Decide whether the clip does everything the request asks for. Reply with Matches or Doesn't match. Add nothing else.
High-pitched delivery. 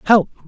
Matches